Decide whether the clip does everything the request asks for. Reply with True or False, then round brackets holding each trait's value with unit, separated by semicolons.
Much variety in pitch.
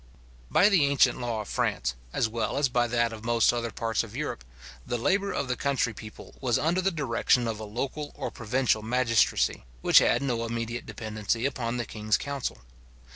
False (3.3 semitones)